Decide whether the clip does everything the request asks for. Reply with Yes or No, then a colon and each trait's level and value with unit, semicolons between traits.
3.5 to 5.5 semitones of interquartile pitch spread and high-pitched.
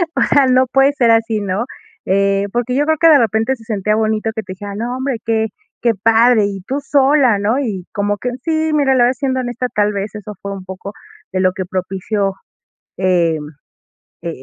Yes: average, 4.4 semitones; high, 220 Hz